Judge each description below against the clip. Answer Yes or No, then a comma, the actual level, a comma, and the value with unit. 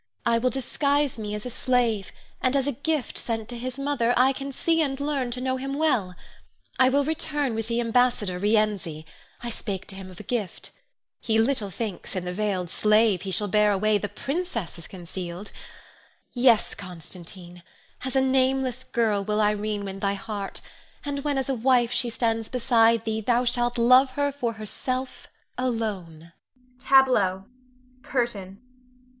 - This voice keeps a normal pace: Yes, average, 170 wpm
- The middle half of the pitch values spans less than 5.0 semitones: Yes, average, 4.3 semitones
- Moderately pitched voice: No, high, 230 Hz